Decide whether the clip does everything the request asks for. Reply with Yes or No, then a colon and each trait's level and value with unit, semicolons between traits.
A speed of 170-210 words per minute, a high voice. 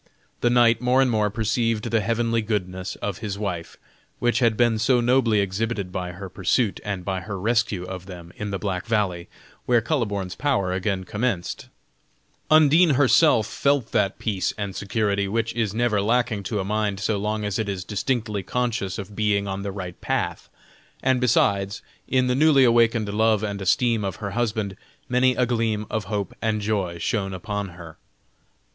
No: average, 175 wpm; low, 105 Hz